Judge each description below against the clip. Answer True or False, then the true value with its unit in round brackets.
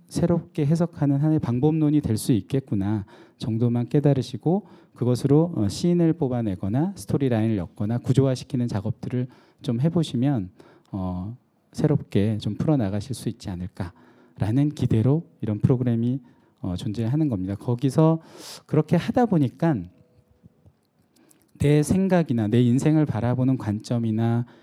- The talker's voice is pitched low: True (125 Hz)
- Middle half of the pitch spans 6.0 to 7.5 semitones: False (5.4 semitones)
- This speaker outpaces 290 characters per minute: True (310 characters per minute)